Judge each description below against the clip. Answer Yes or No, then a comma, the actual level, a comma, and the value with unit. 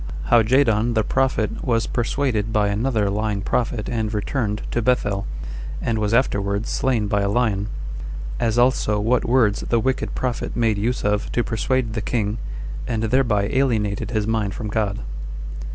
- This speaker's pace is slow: No, average, 160 wpm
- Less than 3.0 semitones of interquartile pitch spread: Yes, narrow, 2.6 semitones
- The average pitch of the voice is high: No, low, 110 Hz